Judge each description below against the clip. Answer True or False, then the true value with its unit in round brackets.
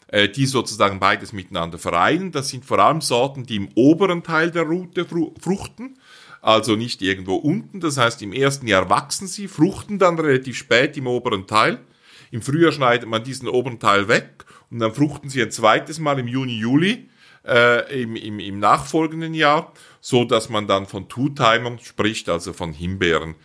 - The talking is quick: False (180 wpm)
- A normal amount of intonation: False (6.9 semitones)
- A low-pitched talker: True (125 Hz)